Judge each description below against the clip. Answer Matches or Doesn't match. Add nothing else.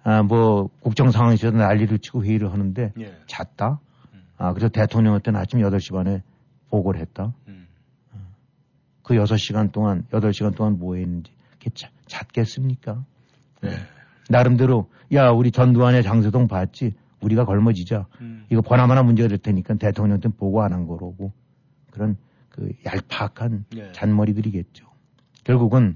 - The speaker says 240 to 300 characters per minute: Matches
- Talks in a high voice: Doesn't match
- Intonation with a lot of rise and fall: Doesn't match